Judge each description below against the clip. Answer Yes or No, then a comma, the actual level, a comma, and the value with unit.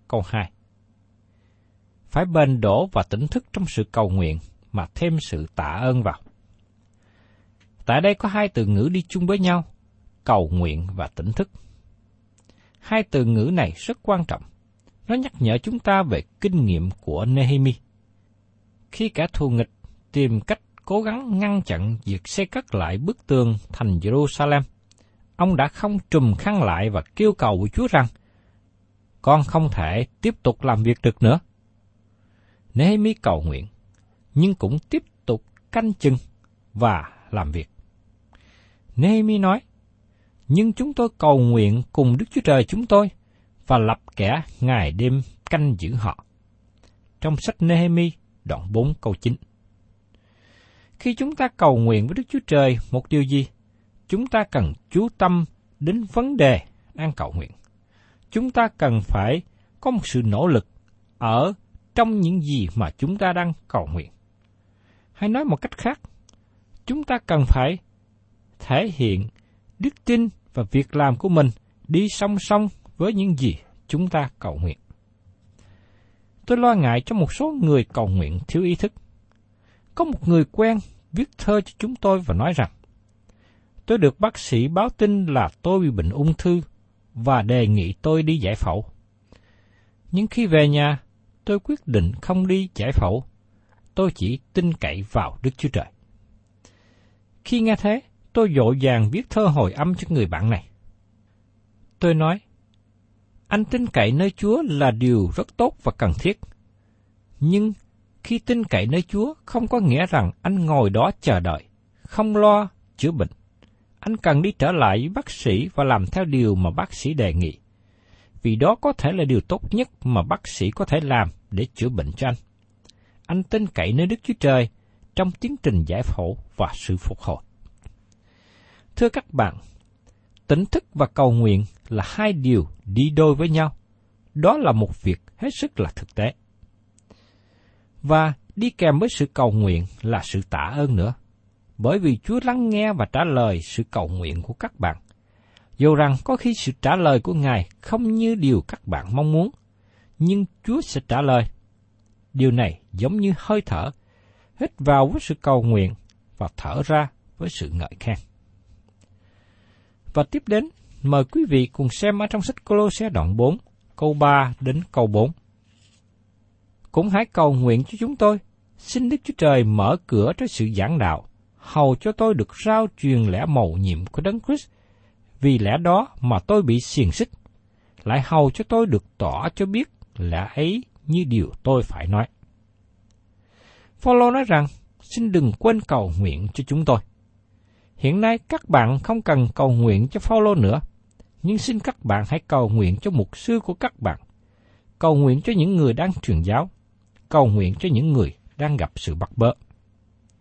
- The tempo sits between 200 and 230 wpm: No, average, 170 wpm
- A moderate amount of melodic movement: No, wide, 8.7 semitones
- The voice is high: No, low, 115 Hz